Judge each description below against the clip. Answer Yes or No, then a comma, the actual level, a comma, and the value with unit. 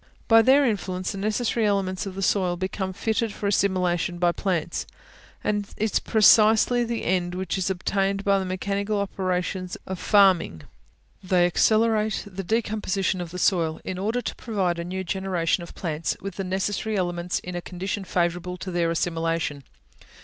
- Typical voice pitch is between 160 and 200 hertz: Yes, high, 190 Hz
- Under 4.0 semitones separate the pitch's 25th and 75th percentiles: Yes, narrow, 2.6 semitones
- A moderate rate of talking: Yes, average, 170 wpm